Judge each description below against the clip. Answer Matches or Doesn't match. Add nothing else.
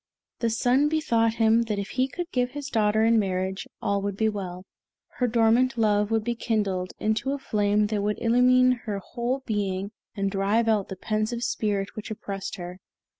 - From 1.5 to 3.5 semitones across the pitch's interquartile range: Matches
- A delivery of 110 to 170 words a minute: Doesn't match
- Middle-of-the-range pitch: Doesn't match